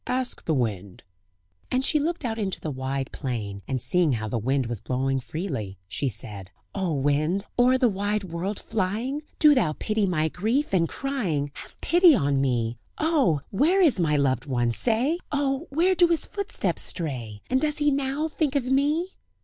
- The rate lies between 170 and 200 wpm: Yes, average, 180 wpm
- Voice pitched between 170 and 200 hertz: Yes, high, 190 Hz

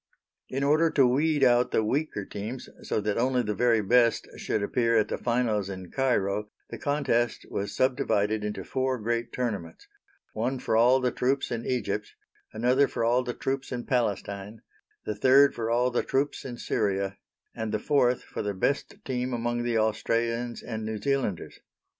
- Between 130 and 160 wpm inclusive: No, average, 175 wpm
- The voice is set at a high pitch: No, low, 120 Hz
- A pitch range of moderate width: Yes, average, 3.1 semitones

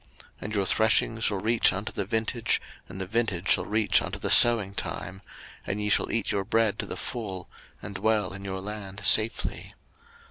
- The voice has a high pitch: No, low, 105 Hz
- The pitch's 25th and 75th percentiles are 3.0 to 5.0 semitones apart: No, narrow, 2.4 semitones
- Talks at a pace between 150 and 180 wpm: No, average, 190 wpm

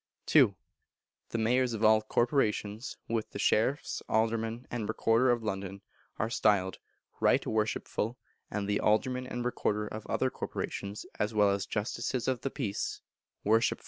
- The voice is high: No, low, 110 Hz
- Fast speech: No, average, 145 wpm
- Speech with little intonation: Yes, narrow, 2.3 semitones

